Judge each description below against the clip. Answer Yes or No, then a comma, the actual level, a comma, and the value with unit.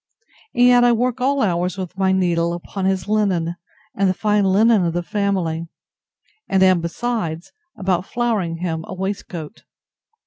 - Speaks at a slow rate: No, average, 160 wpm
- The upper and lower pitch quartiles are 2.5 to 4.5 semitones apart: Yes, average, 3.7 semitones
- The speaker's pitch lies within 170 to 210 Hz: Yes, high, 190 Hz